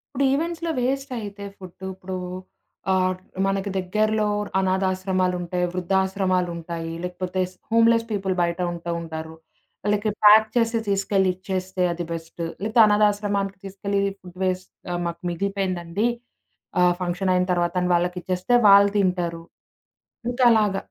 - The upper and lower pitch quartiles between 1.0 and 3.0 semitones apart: Yes, narrow, 2.5 semitones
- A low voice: No, high, 190 Hz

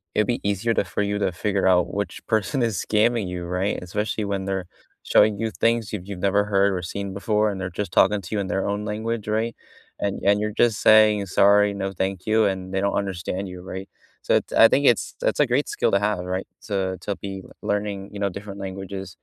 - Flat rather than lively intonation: Yes, narrow, 1.8 semitones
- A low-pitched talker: Yes, low, 100 Hz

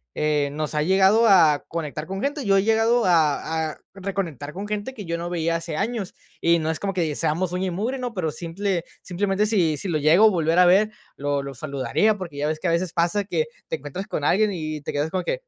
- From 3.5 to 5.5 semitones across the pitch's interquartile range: Yes, average, 4.4 semitones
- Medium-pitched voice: Yes, medium, 175 Hz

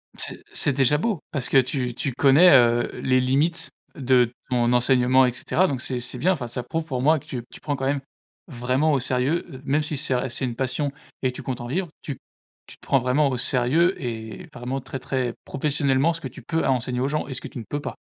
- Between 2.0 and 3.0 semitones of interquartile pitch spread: Yes, average, 2.7 semitones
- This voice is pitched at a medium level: No, low, 130 Hz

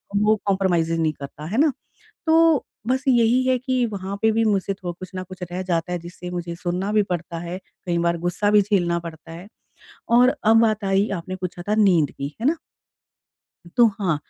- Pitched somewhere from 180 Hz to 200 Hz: Yes, high, 190 Hz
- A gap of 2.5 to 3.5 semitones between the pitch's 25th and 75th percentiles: No, average, 4.2 semitones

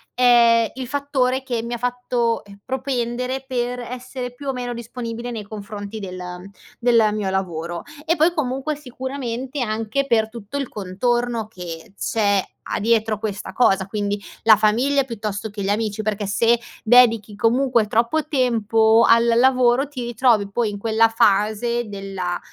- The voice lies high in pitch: Yes, high, 230 Hz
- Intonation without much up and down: No, average, 3.1 semitones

